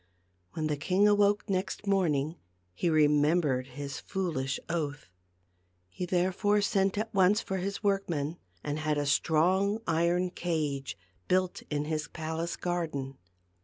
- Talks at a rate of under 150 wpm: Yes, slow, 135 wpm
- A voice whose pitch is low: No, medium, 170 Hz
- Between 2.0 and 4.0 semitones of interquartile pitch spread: No, average, 4.4 semitones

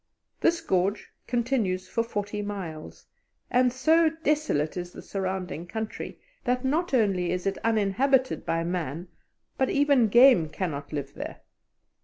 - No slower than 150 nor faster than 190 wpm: No, slow, 135 wpm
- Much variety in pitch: Yes, wide, 6.3 semitones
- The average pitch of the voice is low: No, high, 205 Hz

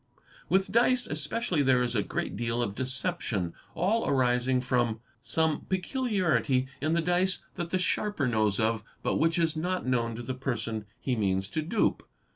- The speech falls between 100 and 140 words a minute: No, average, 180 wpm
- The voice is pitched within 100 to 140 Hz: Yes, low, 135 Hz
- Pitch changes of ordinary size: No, wide, 7.1 semitones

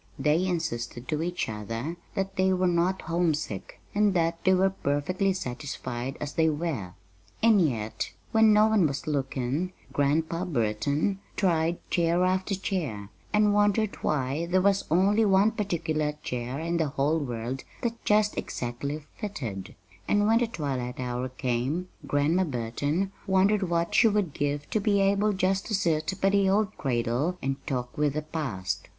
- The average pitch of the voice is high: No, medium, 165 Hz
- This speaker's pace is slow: No, average, 160 wpm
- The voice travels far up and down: Yes, wide, 6.1 semitones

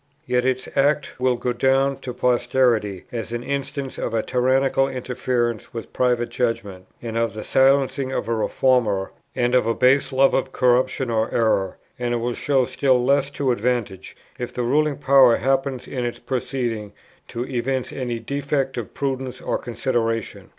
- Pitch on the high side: No, low, 125 Hz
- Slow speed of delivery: No, average, 170 wpm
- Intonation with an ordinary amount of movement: No, narrow, 2.2 semitones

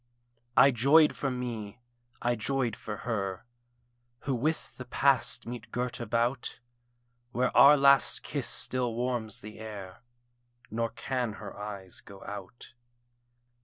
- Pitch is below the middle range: Yes, low, 120 Hz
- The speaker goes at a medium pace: No, slow, 130 wpm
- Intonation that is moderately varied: Yes, average, 3.2 semitones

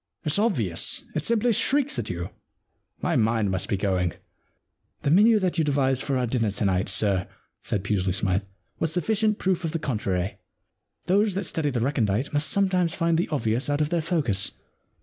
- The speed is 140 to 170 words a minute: No, average, 195 wpm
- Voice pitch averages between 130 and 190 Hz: Yes, medium, 140 Hz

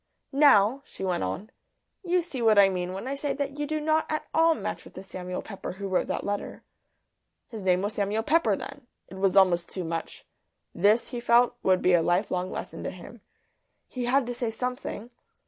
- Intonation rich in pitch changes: Yes, wide, 6.3 semitones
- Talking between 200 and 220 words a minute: Yes, fast, 205 wpm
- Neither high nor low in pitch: No, high, 215 Hz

